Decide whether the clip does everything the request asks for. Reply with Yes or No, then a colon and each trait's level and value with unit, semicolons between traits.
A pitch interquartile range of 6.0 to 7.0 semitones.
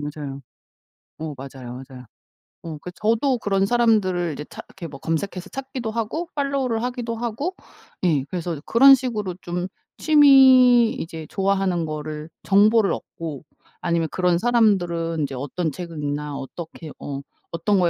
Yes: wide, 6.7 semitones